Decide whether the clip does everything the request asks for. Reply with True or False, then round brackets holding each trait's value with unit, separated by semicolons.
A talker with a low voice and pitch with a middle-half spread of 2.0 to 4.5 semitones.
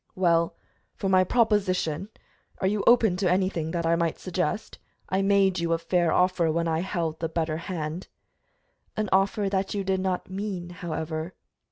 False (180 Hz; 2.6 semitones)